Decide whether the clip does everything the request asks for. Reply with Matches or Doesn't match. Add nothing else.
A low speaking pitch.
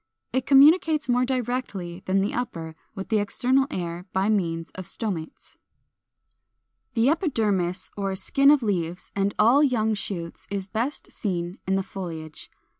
Doesn't match